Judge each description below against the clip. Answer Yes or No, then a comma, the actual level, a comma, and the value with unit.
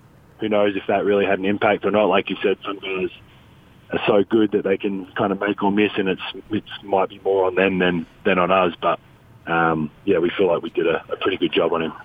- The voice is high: No, low, 100 Hz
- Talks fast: Yes, fast, 265 wpm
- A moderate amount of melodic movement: Yes, average, 3.2 semitones